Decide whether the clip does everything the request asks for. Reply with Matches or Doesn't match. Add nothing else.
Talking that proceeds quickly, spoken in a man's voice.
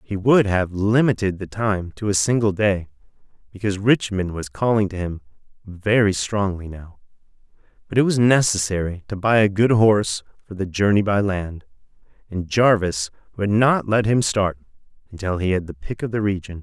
Doesn't match